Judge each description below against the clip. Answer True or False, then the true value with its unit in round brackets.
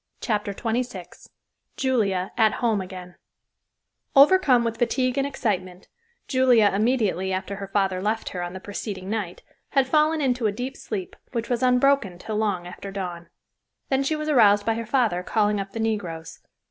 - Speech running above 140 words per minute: True (165 wpm)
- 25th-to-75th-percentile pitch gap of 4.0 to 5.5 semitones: True (4.7 semitones)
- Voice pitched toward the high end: True (215 Hz)